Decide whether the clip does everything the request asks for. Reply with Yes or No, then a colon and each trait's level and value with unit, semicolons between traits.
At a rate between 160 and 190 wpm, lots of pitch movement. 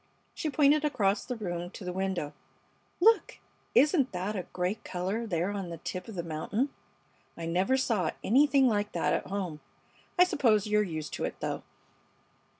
Yes: average, 170 wpm; wide, 6.0 semitones